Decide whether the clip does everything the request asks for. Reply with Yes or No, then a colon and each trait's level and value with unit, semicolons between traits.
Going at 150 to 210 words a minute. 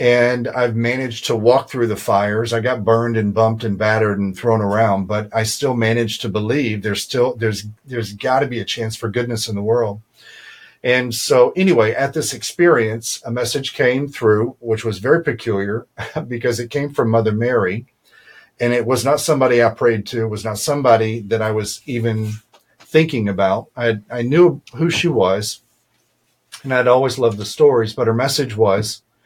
Yes: average, 190 wpm